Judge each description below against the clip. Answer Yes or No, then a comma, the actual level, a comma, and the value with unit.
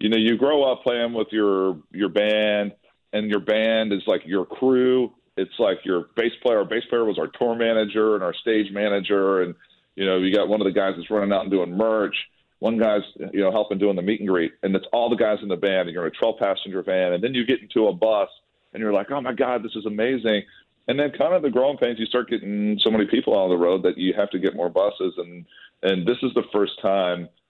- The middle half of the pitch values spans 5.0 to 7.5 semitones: No, average, 3.4 semitones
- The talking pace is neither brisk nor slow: No, fast, 260 wpm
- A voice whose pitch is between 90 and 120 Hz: Yes, low, 105 Hz